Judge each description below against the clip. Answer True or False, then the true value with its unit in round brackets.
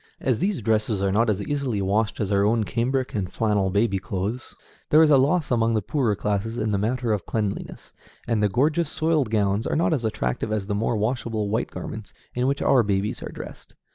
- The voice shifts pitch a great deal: False (3.8 semitones)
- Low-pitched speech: True (110 Hz)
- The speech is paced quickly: True (215 wpm)